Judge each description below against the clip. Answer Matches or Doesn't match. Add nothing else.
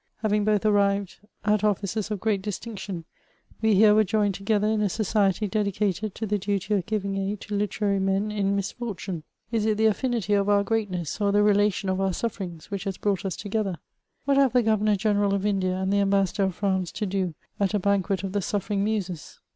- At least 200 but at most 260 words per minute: Matches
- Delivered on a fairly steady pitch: Matches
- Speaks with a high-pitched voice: Matches